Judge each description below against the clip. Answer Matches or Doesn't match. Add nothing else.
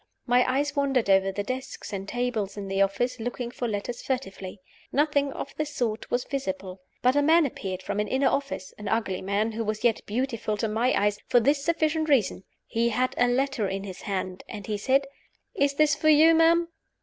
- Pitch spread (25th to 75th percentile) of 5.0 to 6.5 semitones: Matches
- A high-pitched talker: Matches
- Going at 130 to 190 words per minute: Doesn't match